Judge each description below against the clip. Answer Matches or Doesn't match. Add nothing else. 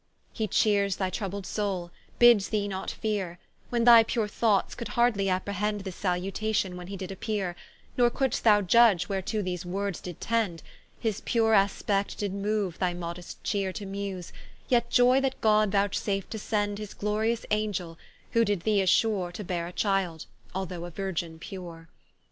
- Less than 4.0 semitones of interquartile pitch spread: Matches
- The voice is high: Matches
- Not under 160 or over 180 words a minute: Matches